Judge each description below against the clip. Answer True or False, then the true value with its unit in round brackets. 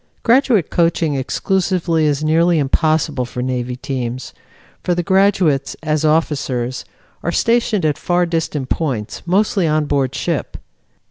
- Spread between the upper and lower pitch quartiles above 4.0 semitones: True (4.5 semitones)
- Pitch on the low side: False (155 Hz)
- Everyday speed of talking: False (130 wpm)